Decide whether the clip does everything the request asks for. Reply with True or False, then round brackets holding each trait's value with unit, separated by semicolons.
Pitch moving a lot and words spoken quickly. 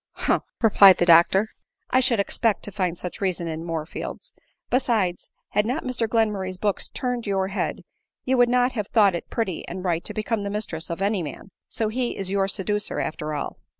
False (4.0 semitones; 210 wpm)